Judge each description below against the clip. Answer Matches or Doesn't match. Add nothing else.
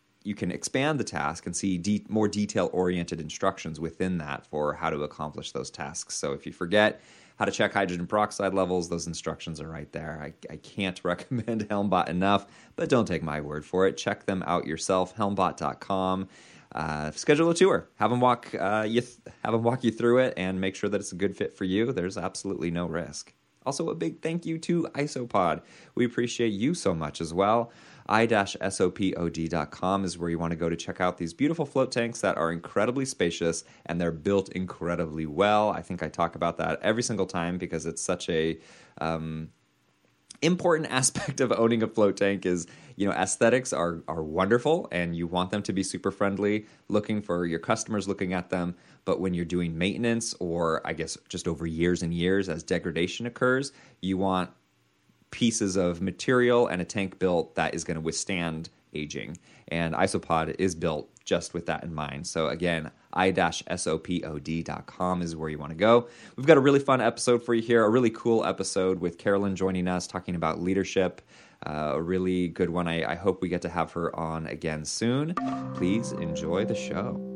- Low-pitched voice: Matches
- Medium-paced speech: Matches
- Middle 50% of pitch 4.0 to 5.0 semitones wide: Matches